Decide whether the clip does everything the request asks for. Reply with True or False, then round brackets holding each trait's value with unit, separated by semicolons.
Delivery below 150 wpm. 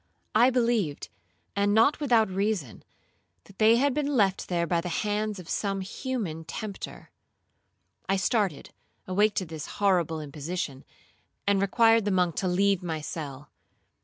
True (140 wpm)